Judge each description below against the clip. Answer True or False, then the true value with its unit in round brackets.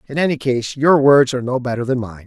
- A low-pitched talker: True (130 Hz)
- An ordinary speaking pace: False (265 wpm)